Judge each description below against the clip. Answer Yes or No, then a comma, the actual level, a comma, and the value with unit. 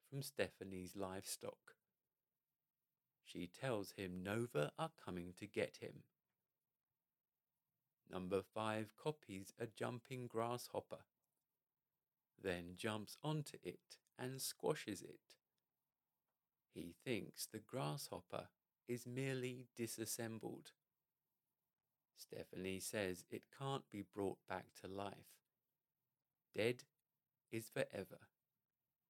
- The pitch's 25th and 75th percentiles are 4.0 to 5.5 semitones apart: Yes, average, 4.8 semitones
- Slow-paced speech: Yes, slow, 90 wpm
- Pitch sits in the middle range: No, low, 110 Hz